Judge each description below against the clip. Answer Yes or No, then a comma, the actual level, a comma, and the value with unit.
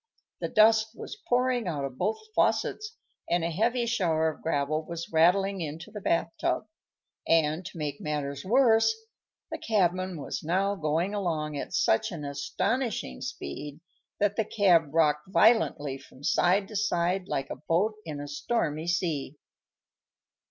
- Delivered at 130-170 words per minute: Yes, average, 150 wpm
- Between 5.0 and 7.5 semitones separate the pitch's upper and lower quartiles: Yes, wide, 5.5 semitones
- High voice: No, medium, 175 Hz